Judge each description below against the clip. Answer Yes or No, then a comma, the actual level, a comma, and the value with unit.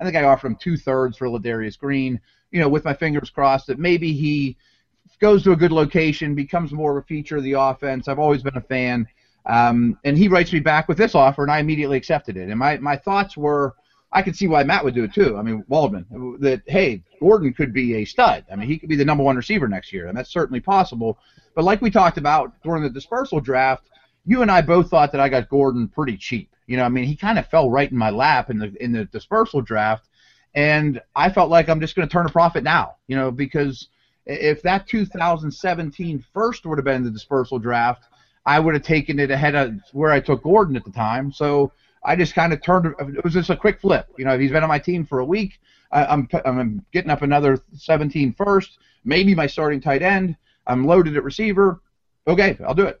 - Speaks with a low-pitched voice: No, medium, 145 Hz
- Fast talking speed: Yes, fast, 240 wpm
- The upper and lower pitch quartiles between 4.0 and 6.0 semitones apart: Yes, average, 4.5 semitones